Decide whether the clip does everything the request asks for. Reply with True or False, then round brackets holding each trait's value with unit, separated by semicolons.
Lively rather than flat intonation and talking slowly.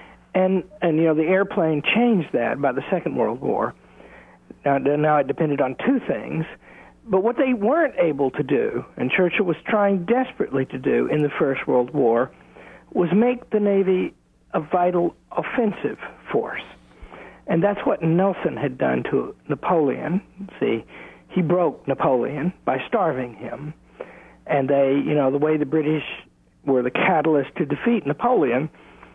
False (5.9 semitones; 155 wpm)